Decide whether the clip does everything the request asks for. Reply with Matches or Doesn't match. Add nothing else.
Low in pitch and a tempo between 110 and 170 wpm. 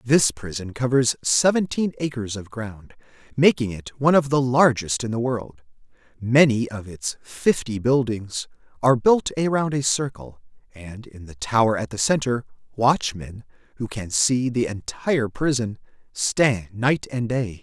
Matches